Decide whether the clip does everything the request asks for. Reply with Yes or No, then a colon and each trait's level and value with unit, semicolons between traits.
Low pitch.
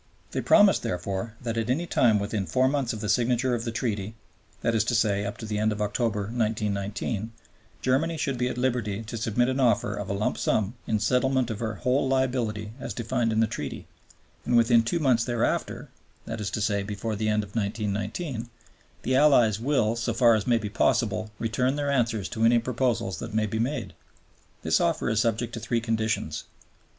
Yes: low, 115 Hz